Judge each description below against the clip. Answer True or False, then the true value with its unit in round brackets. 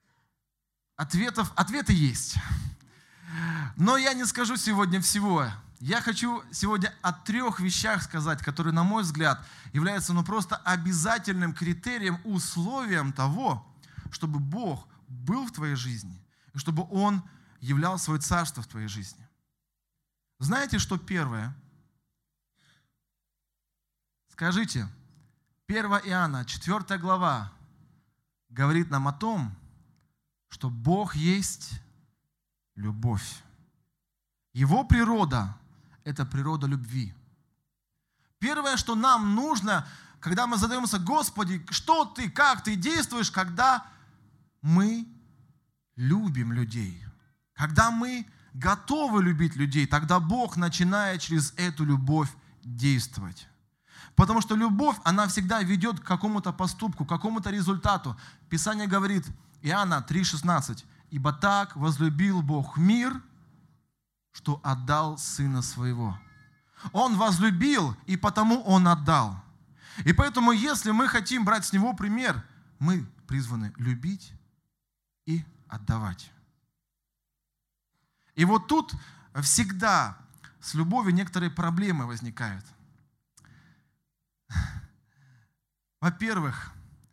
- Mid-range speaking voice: True (160 Hz)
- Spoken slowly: True (100 wpm)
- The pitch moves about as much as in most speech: False (6.2 semitones)